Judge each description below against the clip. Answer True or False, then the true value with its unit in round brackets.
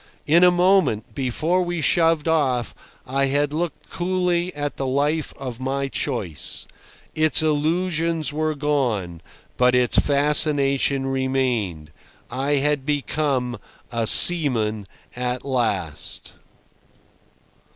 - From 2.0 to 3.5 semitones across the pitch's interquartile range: False (3.9 semitones)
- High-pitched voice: False (140 Hz)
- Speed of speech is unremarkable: False (110 wpm)